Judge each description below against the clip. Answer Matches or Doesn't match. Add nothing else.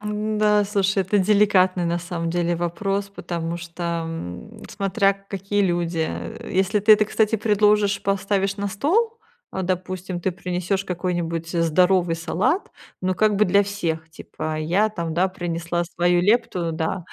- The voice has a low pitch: Doesn't match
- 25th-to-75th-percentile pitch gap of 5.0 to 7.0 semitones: Doesn't match